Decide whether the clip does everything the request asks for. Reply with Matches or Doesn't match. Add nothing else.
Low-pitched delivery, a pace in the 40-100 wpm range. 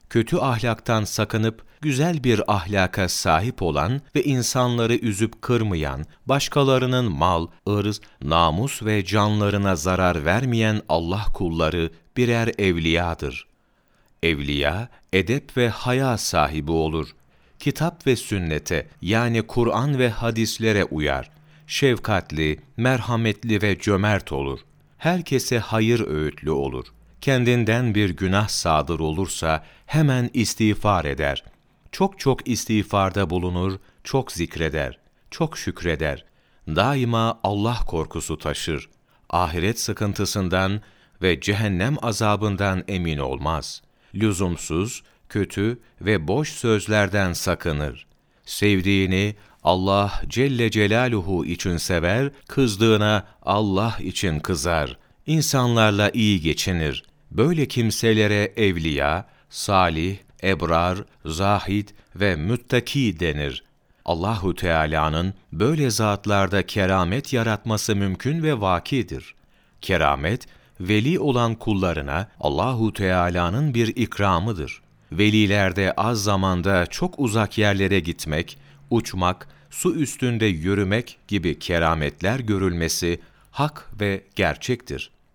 Matches